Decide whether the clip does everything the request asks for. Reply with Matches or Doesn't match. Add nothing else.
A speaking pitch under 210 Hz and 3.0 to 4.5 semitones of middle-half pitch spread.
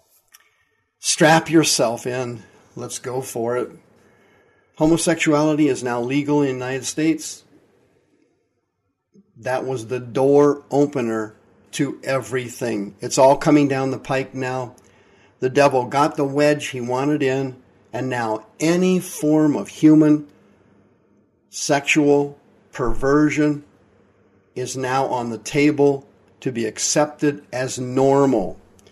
Matches